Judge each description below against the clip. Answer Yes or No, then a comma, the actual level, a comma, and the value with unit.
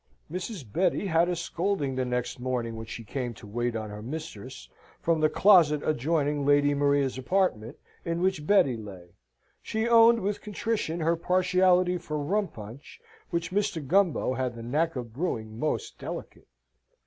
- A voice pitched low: No, medium, 150 Hz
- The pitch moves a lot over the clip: Yes, wide, 6.6 semitones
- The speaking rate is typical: Yes, average, 160 wpm